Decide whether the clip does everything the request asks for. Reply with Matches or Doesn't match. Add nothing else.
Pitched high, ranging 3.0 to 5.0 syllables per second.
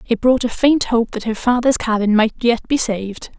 Doesn't match